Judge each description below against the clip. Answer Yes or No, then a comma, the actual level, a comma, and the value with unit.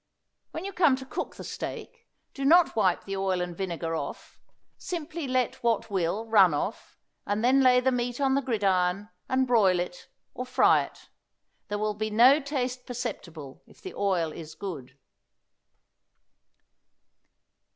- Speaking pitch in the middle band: No, high, 225 Hz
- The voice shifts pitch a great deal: Yes, wide, 6.0 semitones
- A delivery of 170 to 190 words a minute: No, average, 155 wpm